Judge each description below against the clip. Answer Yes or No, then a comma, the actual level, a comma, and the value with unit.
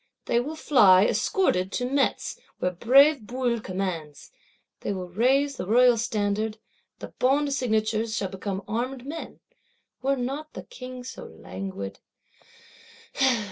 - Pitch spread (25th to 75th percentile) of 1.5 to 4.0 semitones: No, wide, 5.4 semitones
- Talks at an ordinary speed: No, slow, 130 wpm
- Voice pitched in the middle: No, high, 230 Hz